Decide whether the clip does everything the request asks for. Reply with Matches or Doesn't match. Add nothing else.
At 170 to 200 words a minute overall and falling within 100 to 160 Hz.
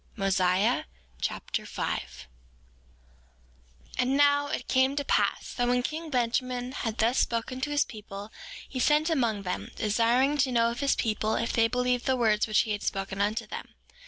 Doesn't match